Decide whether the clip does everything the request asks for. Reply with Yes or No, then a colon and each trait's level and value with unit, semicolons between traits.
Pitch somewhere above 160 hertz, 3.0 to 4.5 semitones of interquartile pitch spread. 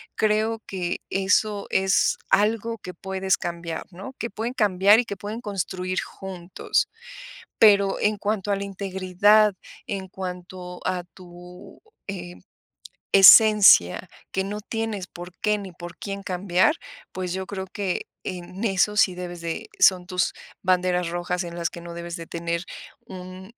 No: high, 190 Hz; narrow, 2.4 semitones